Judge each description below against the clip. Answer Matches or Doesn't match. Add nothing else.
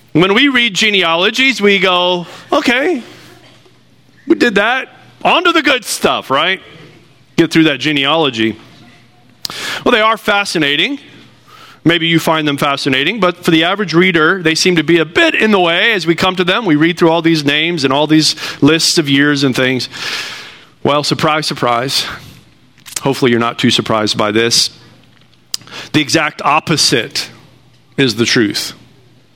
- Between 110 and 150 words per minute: Doesn't match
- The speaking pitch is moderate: Matches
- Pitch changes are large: Doesn't match